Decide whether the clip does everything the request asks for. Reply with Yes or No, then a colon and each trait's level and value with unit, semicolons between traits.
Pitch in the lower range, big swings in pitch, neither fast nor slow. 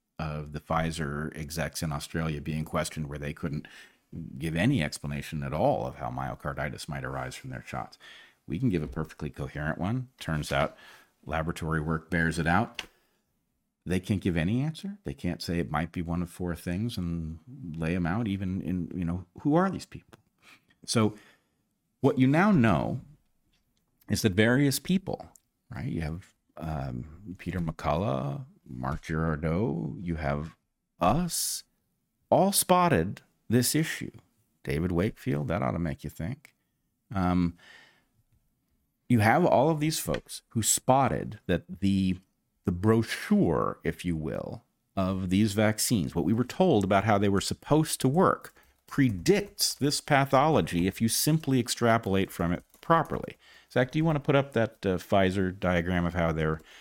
Yes: very low, 90 Hz; wide, 7.2 semitones; average, 160 wpm